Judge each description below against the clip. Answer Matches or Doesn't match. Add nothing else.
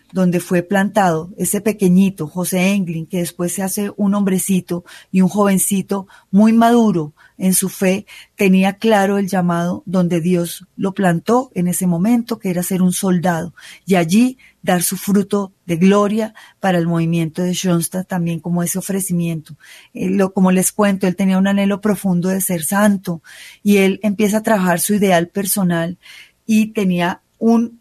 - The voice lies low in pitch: Doesn't match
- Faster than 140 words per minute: Matches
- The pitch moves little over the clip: Matches